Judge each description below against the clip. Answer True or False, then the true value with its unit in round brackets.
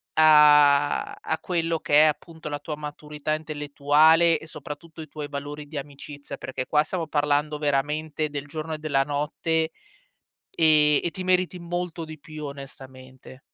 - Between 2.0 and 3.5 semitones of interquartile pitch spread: False (1.5 semitones)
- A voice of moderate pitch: True (150 Hz)